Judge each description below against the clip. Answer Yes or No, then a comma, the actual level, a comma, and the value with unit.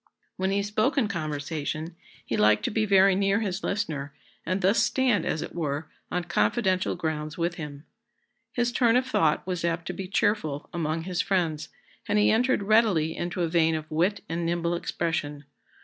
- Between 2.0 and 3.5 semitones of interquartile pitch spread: No, average, 4.3 semitones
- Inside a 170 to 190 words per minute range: Yes, average, 180 wpm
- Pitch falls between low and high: Yes, medium, 175 Hz